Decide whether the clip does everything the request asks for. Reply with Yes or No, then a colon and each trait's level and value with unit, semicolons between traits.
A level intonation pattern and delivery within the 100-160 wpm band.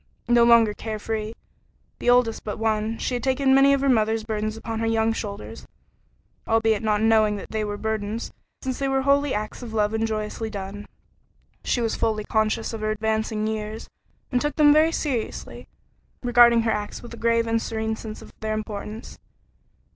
No: narrow, 1.6 semitones; average, 185 wpm